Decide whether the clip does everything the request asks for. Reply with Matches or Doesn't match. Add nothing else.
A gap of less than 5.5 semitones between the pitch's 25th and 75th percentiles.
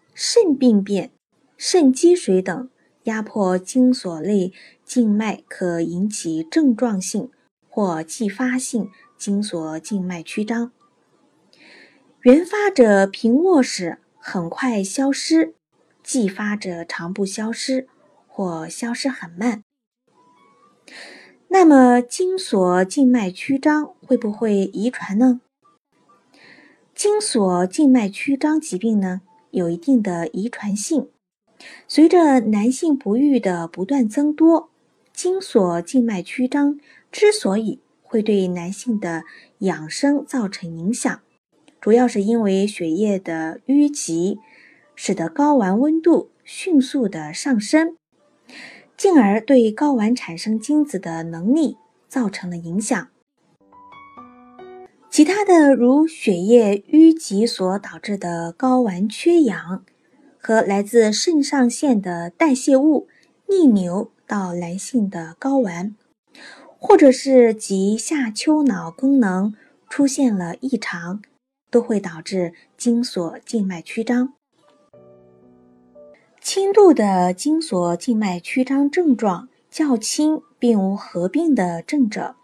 Doesn't match